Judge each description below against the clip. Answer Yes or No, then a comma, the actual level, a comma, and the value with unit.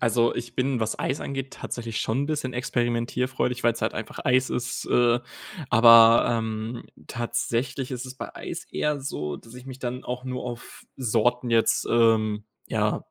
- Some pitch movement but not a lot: No, narrow, 1.8 semitones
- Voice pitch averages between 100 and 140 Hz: Yes, low, 120 Hz